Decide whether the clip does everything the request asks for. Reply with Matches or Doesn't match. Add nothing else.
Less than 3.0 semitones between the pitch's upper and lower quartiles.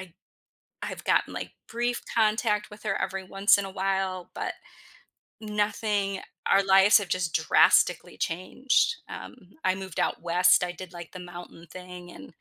Matches